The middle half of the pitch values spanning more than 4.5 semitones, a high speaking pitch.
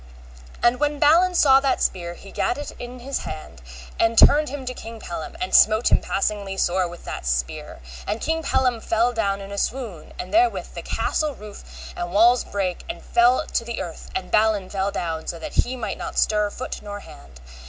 Yes: average, 5.2 semitones; high, 220 Hz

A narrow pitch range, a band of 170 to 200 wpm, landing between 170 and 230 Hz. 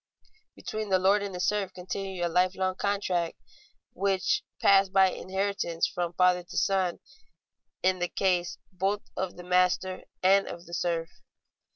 No: narrow, 1.6 semitones; average, 150 wpm; medium, 185 Hz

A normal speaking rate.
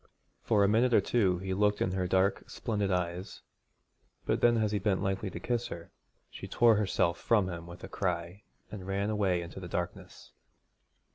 Yes: average, 190 wpm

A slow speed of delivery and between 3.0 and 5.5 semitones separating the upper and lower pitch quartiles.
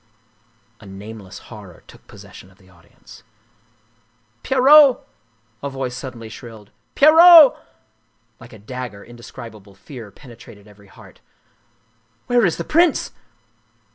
Yes: slow, 130 wpm; average, 4.2 semitones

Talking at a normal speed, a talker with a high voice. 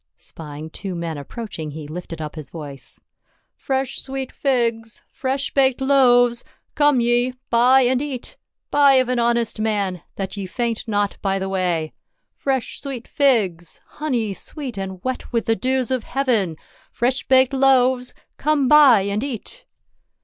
Yes: average, 160 wpm; high, 240 Hz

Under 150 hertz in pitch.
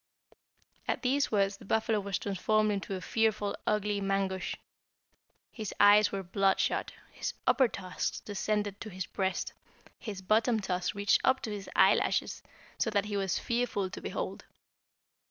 No: high, 205 Hz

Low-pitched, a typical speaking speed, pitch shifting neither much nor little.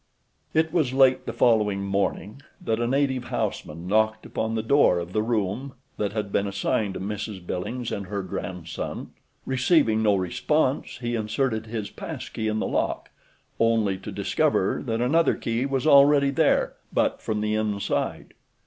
Yes: low, 110 Hz; average, 165 wpm; average, 4.3 semitones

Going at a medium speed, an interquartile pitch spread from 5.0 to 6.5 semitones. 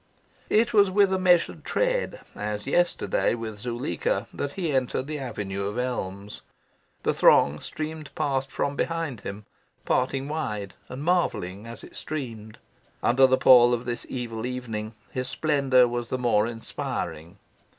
Yes: average, 150 wpm; wide, 5.4 semitones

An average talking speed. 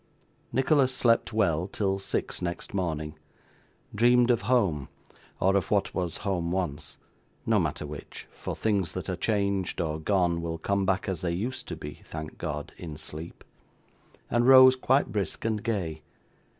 Yes: average, 160 wpm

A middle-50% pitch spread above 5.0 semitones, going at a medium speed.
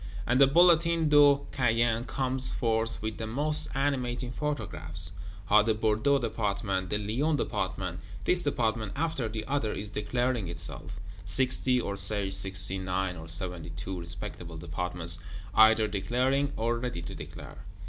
Yes: wide, 5.4 semitones; average, 145 wpm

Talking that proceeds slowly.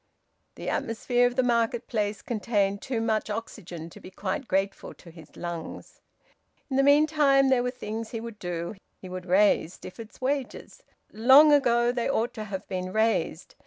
No: average, 165 wpm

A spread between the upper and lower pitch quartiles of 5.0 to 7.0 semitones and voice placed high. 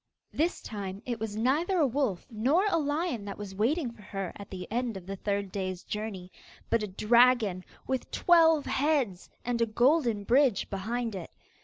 Yes: wide, 5.5 semitones; high, 230 Hz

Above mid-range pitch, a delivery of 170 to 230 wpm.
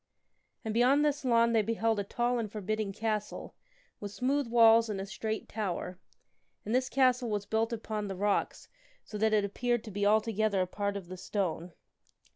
Yes: high, 220 Hz; average, 185 wpm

